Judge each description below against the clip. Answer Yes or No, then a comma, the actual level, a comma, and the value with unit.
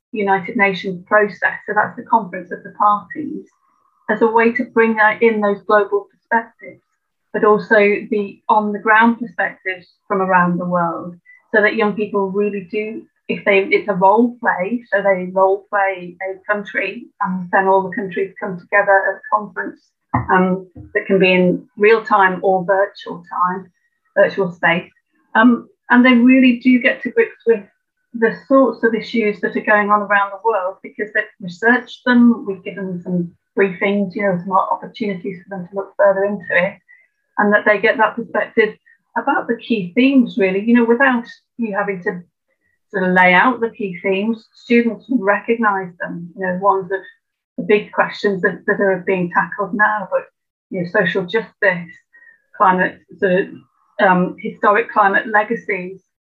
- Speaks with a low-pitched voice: No, high, 210 Hz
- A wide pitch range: No, average, 3.0 semitones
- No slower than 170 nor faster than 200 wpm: Yes, average, 175 wpm